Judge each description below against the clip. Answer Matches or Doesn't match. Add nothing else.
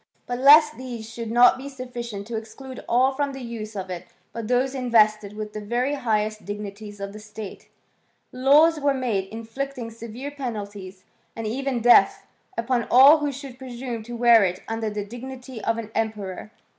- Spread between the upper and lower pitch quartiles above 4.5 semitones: Doesn't match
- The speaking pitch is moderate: Doesn't match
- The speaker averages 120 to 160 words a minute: Doesn't match